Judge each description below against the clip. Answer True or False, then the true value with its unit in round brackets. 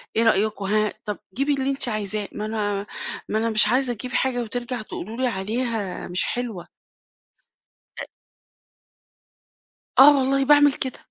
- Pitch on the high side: True (230 Hz)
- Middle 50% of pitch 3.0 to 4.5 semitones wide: True (3.6 semitones)